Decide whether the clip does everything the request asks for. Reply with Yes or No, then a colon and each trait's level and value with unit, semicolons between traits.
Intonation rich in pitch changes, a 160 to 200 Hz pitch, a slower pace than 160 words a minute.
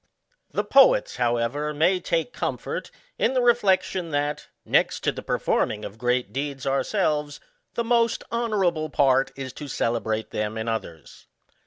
No: wide, 7.8 semitones; medium, 145 Hz; average, 150 wpm